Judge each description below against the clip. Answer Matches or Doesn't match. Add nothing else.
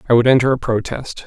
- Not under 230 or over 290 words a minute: Matches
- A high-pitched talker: Doesn't match